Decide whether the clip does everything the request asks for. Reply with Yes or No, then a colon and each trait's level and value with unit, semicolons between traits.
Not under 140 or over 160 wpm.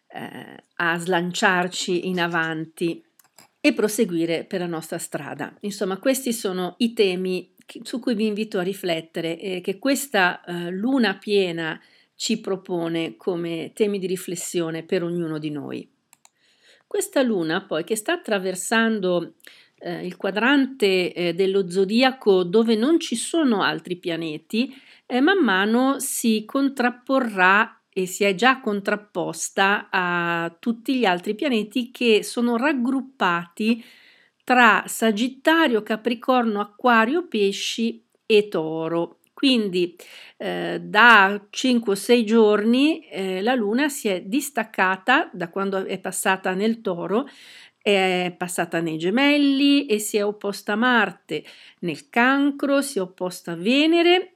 No: average, 130 wpm